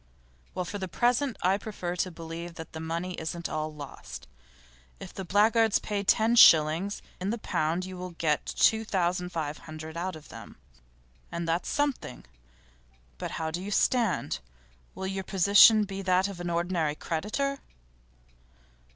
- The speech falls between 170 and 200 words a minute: No, average, 160 wpm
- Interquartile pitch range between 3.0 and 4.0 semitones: Yes, average, 3.7 semitones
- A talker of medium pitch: Yes, medium, 180 Hz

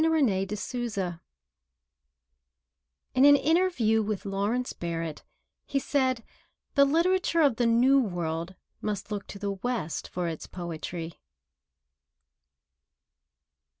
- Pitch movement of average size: No, wide, 6.9 semitones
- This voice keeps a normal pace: No, slow, 110 wpm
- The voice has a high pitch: Yes, high, 220 Hz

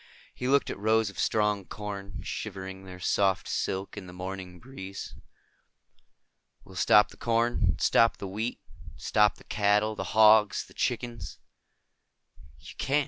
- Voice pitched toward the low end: Yes, low, 105 Hz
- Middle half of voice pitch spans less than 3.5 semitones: Yes, narrow, 2.6 semitones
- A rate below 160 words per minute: Yes, average, 140 wpm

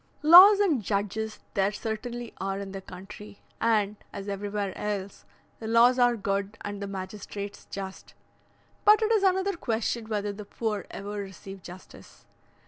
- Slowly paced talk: No, average, 150 wpm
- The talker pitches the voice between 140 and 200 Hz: No, high, 210 Hz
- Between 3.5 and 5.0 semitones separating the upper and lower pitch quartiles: No, average, 2.9 semitones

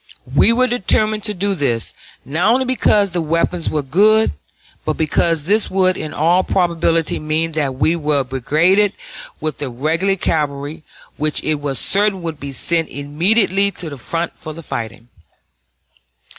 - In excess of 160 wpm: No, average, 155 wpm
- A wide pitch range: No, average, 4.7 semitones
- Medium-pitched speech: Yes, medium, 165 Hz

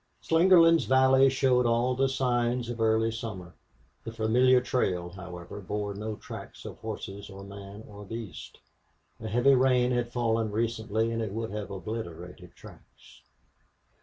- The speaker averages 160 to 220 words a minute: No, average, 145 wpm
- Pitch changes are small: No, average, 3.6 semitones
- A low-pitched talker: Yes, low, 115 Hz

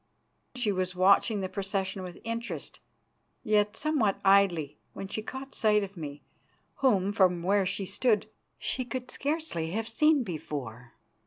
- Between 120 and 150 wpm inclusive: Yes, average, 145 wpm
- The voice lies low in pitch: No, high, 200 Hz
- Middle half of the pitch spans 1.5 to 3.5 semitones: No, average, 3.9 semitones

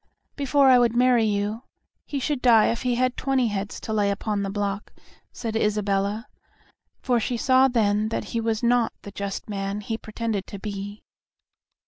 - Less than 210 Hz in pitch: No, high, 220 Hz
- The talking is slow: No, average, 175 wpm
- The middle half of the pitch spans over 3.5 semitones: No, average, 3.2 semitones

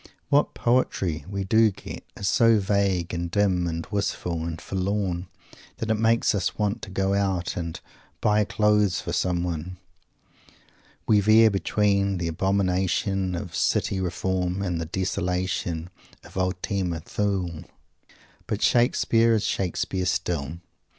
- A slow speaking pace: Yes, slow, 130 wpm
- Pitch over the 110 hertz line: No, very low, 95 Hz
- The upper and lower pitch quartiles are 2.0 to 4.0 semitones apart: Yes, average, 2.7 semitones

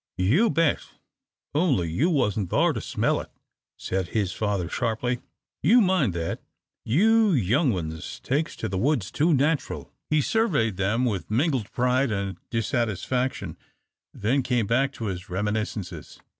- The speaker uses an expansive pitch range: Yes, wide, 6.7 semitones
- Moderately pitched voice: No, low, 120 Hz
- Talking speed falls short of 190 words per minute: Yes, average, 145 wpm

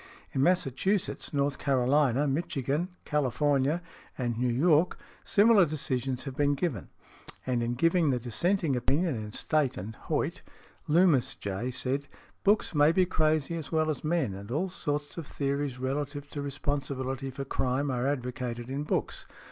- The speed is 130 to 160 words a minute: Yes, average, 150 wpm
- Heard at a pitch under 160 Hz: Yes, medium, 140 Hz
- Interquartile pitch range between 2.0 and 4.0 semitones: Yes, average, 3.4 semitones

